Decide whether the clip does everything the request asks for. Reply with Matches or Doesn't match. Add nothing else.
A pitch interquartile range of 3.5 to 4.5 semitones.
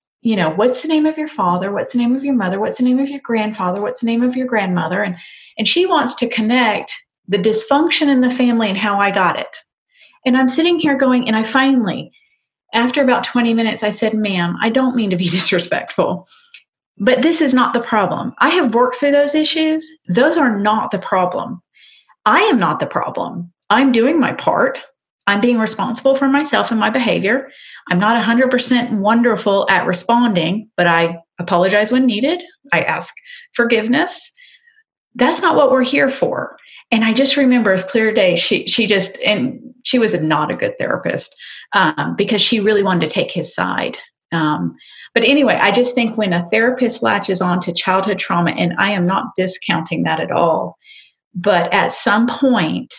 Doesn't match